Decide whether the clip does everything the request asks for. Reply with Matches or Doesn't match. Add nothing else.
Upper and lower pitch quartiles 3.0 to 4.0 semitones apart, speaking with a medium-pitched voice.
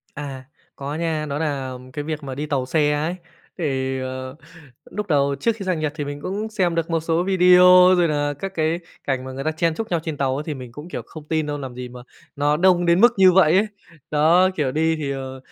Matches